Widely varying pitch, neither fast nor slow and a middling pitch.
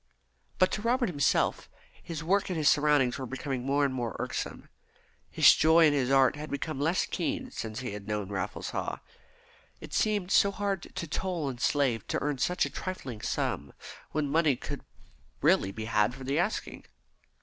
Yes: wide, 5.9 semitones; average, 185 wpm; medium, 145 Hz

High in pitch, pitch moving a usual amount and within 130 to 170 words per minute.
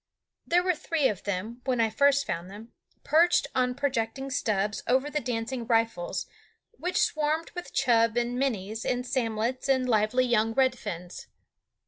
Yes: high, 245 Hz; average, 3.6 semitones; average, 155 wpm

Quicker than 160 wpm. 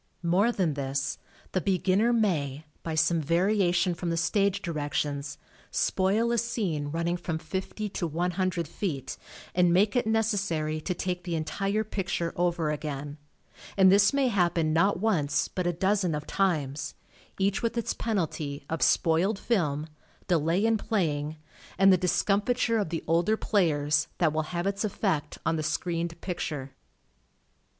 No: average, 155 wpm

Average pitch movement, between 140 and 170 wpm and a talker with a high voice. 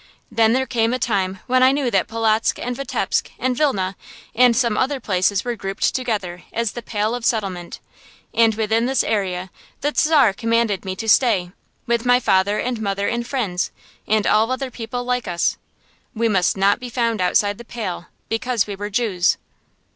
No: average, 3.7 semitones; average, 185 wpm; high, 225 Hz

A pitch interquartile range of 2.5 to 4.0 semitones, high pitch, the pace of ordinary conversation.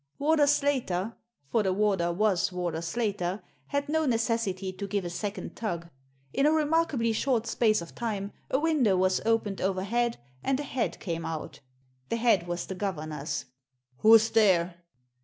No: average, 4.8 semitones; high, 210 Hz; average, 160 wpm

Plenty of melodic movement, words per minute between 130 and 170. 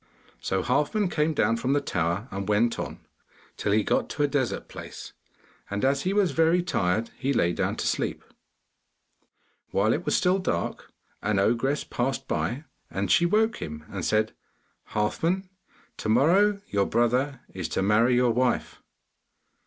Yes: wide, 7.1 semitones; average, 160 wpm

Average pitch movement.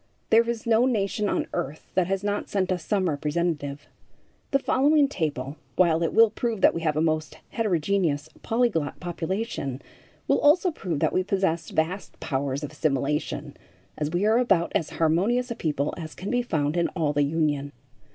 No: wide, 5.9 semitones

